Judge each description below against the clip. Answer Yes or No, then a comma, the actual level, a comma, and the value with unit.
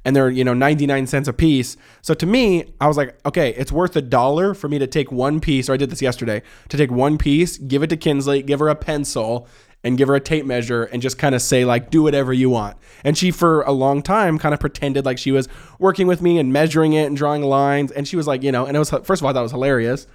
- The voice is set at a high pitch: No, medium, 140 Hz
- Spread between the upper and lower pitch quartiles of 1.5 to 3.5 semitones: Yes, average, 2.7 semitones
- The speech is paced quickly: Yes, fast, 285 wpm